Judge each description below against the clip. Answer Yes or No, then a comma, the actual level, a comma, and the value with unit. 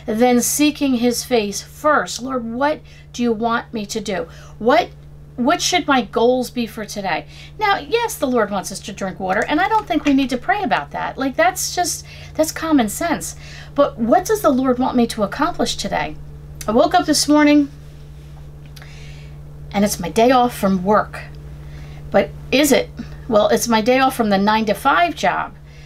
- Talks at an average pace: Yes, average, 190 wpm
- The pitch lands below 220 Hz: No, high, 230 Hz